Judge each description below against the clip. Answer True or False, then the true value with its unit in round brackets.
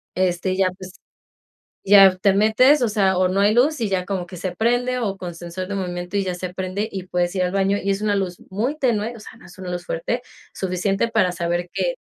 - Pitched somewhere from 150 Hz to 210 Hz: True (190 Hz)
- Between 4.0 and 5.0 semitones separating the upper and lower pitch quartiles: False (2.8 semitones)